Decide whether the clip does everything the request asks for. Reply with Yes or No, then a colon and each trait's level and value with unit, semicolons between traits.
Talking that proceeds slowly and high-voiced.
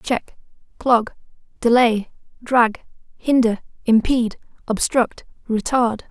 Yes: slow, 80 wpm; high, 235 Hz